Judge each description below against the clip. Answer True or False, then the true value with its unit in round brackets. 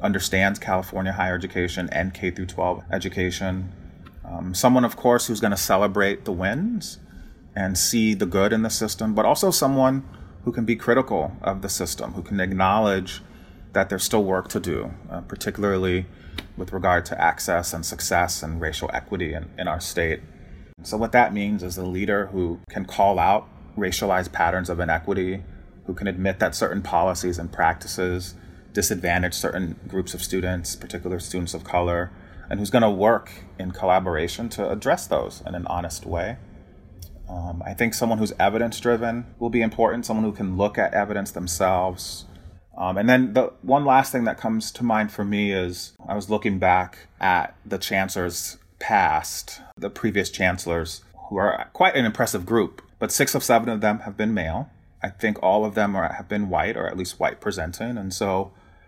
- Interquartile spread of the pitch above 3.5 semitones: False (3.2 semitones)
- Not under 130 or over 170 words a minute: False (180 wpm)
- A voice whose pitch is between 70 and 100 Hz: True (95 Hz)